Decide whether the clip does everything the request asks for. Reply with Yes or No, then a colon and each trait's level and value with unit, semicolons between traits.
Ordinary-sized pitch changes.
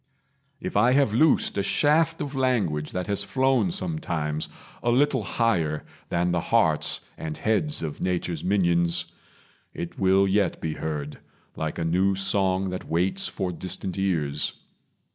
No: wide, 5.8 semitones